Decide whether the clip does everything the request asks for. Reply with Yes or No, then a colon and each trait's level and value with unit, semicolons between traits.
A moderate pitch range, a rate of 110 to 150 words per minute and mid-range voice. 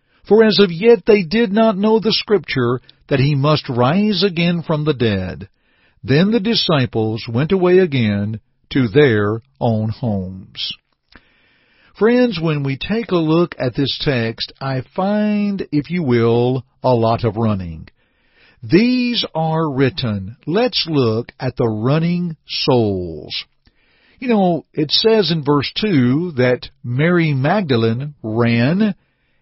No: wide, 7.8 semitones; slow, 135 wpm; medium, 145 Hz